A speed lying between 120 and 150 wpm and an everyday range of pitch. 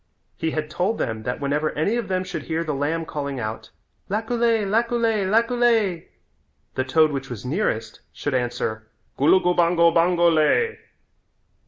No: average, 145 wpm; wide, 6.7 semitones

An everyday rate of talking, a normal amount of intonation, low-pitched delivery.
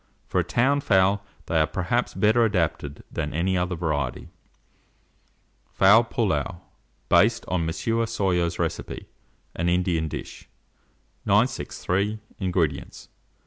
No: slow, 110 wpm; average, 4.3 semitones; very low, 90 Hz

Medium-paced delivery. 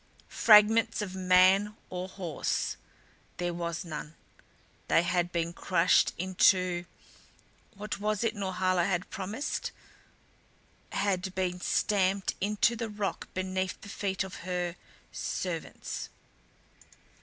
No: slow, 110 wpm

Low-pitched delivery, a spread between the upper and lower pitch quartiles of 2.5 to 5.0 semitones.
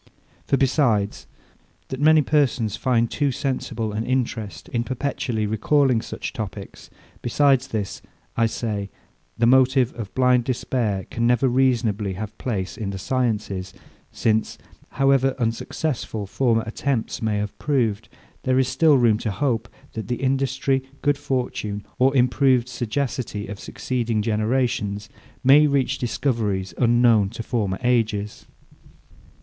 Yes: low, 120 Hz; average, 3.6 semitones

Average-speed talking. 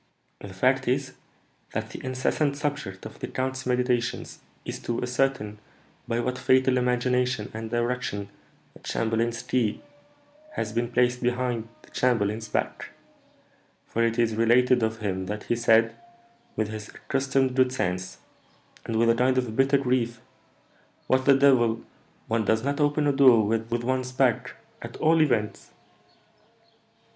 Yes: average, 145 wpm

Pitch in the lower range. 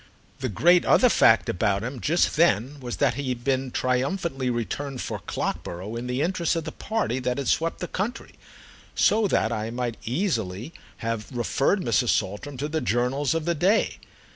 Yes: low, 130 Hz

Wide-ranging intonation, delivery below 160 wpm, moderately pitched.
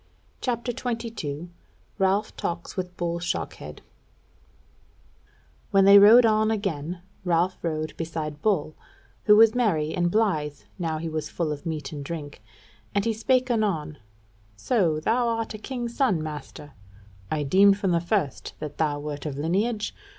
Yes: wide, 5.8 semitones; average, 150 wpm; medium, 175 Hz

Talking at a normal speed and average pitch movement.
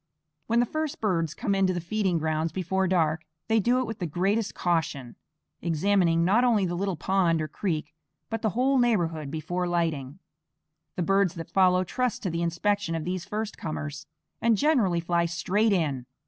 Yes: average, 185 wpm; average, 3.9 semitones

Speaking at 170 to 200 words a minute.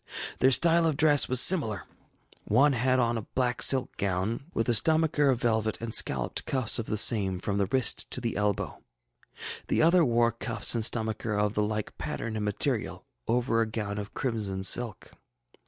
Yes: average, 185 wpm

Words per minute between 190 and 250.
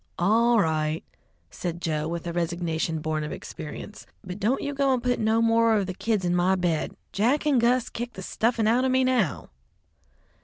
Yes: average, 195 wpm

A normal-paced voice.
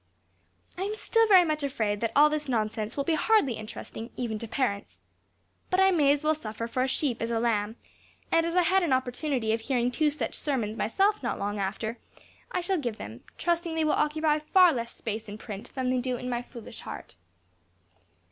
No: fast, 210 wpm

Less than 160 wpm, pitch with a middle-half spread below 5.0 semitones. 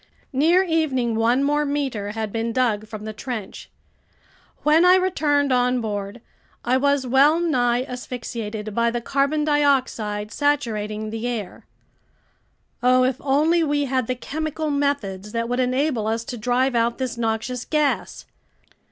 Yes: average, 145 wpm; average, 4.2 semitones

